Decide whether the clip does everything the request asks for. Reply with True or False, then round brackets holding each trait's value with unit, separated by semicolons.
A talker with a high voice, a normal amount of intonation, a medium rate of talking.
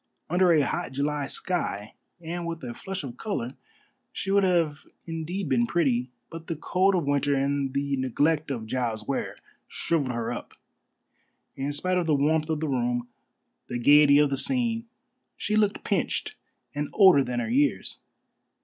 False (145 Hz; 4.8 semitones; 165 wpm)